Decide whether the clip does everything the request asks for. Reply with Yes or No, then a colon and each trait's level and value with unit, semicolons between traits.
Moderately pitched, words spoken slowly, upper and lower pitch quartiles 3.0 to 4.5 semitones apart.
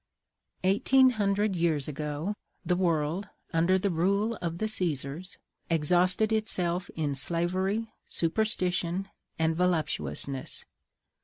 Yes: medium, 180 Hz; slow, 100 wpm; average, 3.4 semitones